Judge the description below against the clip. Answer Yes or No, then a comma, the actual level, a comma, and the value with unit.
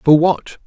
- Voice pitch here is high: No, medium, 160 Hz